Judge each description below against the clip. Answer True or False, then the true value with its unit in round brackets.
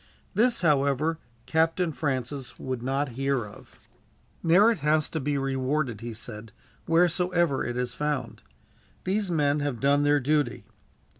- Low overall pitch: False (145 Hz)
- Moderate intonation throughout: True (3.9 semitones)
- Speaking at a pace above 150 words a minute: False (135 wpm)